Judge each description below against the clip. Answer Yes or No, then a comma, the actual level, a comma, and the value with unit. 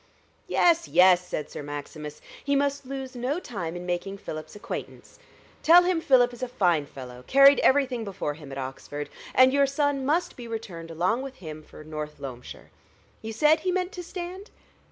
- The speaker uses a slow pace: No, average, 180 wpm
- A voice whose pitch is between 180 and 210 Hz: No, high, 230 Hz